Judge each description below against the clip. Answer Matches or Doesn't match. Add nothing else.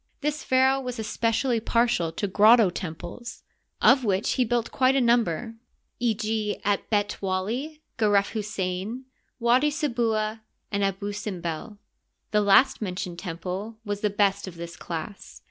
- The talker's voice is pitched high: Matches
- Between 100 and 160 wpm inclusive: Matches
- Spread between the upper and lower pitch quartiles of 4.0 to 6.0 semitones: Doesn't match